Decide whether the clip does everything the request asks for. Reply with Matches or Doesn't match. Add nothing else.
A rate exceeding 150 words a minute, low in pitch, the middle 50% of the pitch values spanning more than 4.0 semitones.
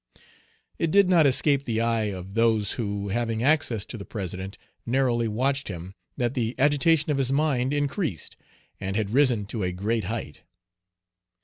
Matches